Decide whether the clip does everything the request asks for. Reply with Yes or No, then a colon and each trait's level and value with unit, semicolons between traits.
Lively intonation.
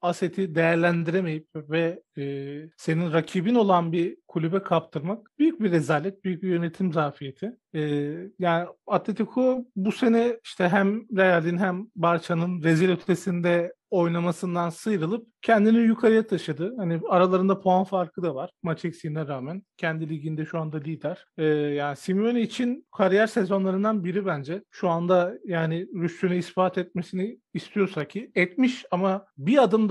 No: average, 3.2 semitones